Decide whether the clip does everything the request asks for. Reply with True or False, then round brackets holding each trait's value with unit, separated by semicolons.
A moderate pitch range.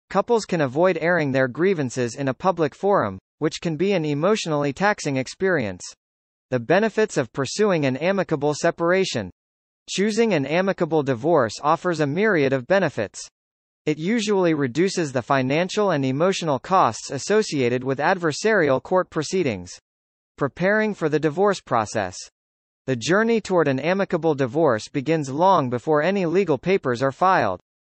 False (6.0 semitones)